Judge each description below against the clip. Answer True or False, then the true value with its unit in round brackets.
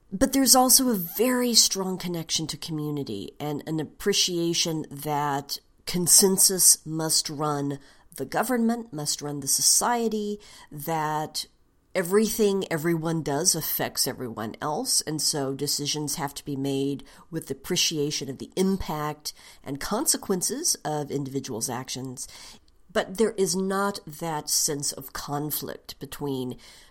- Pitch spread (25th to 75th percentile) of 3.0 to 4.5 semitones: False (5.0 semitones)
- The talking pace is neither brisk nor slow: False (125 wpm)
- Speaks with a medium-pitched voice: True (155 Hz)